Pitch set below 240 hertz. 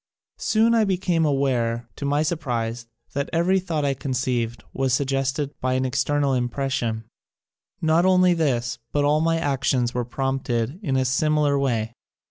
Yes: low, 135 Hz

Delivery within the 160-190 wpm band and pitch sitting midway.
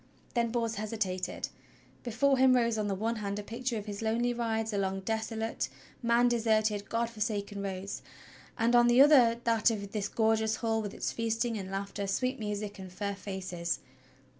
No: average, 175 wpm; high, 220 Hz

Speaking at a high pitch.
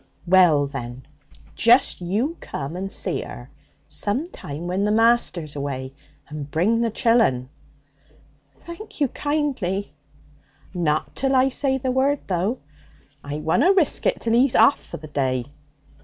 Yes: high, 195 Hz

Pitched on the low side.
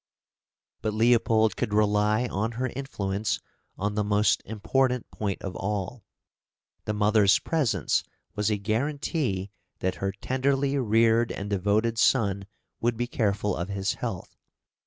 Yes: low, 105 Hz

